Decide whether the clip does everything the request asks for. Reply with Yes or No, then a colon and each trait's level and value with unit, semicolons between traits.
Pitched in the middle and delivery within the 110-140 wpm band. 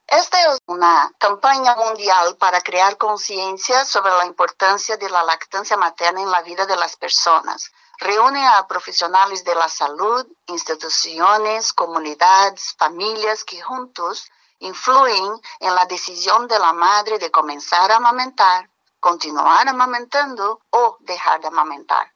No: high, 200 Hz; slow, 135 wpm